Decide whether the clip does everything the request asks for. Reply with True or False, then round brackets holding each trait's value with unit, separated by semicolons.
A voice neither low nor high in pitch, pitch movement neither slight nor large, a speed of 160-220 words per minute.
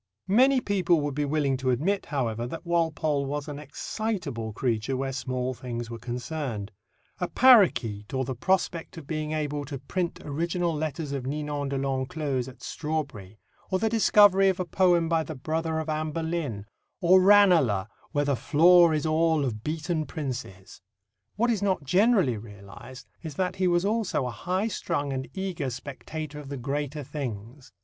True (150 Hz; 4.8 semitones; 170 wpm)